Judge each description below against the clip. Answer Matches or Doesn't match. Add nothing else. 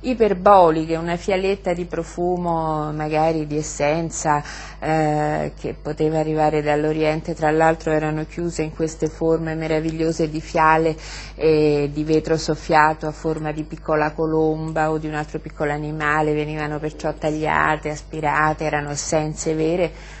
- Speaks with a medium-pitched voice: Matches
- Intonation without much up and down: Matches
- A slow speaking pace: Doesn't match